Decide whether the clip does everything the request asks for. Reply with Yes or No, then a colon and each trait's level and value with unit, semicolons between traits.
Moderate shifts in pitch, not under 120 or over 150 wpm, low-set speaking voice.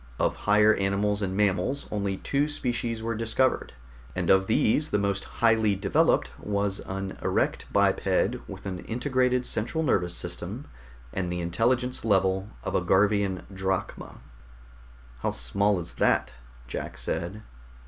Yes: average, 3.1 semitones; average, 140 wpm; low, 100 Hz